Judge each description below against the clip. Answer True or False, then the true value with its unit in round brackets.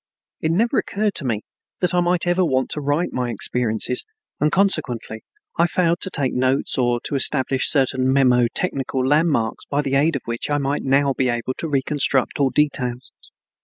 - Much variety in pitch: False (3.9 semitones)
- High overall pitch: False (135 Hz)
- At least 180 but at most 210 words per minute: True (185 wpm)